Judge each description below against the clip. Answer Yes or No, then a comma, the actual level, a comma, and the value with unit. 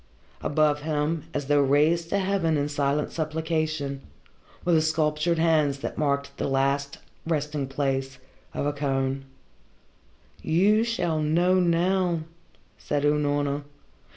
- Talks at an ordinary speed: No, slow, 125 wpm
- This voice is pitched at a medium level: Yes, medium, 150 Hz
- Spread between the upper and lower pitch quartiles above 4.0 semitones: No, narrow, 2.6 semitones